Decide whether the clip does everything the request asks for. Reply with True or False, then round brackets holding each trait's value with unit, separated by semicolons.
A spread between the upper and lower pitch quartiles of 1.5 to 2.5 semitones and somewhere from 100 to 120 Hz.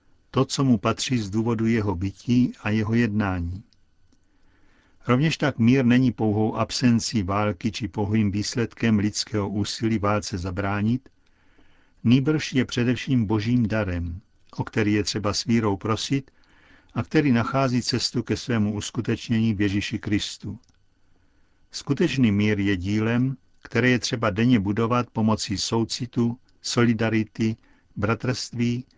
False (2.9 semitones; 110 Hz)